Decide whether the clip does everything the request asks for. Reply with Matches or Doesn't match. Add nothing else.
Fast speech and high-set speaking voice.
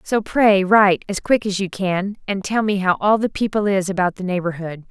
Matches